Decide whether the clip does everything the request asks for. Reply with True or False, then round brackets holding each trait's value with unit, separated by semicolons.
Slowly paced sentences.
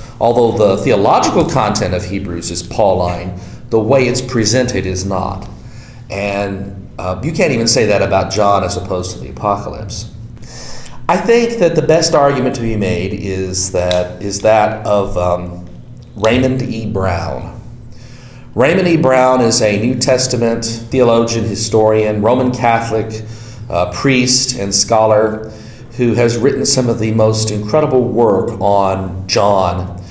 False (145 wpm)